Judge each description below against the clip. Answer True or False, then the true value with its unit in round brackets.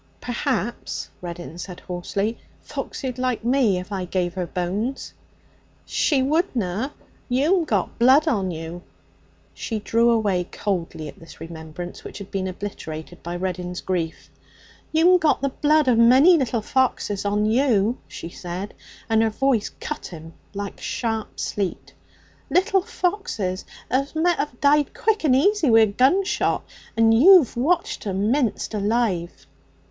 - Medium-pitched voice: False (225 Hz)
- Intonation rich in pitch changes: True (7.0 semitones)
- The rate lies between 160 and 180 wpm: False (145 wpm)